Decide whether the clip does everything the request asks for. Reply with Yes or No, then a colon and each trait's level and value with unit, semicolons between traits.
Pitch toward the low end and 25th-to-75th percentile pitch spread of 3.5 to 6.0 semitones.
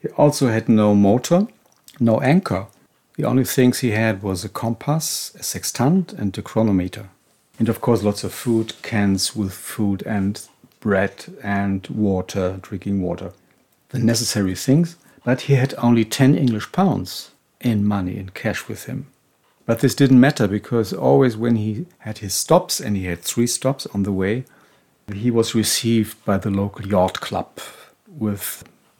Yes: low, 110 Hz; average, 4.0 semitones